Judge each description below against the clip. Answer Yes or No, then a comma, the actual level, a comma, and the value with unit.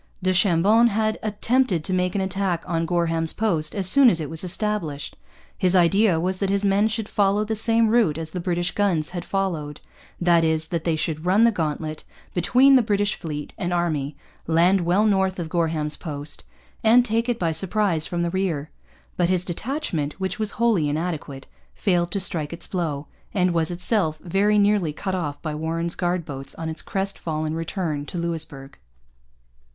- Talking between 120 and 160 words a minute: No, average, 185 wpm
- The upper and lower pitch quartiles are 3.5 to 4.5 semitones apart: Yes, average, 3.9 semitones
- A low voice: No, medium, 175 Hz